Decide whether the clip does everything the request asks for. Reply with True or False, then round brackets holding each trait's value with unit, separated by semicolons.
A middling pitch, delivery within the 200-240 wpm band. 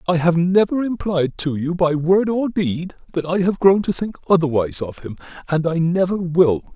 True (175 Hz; 205 wpm)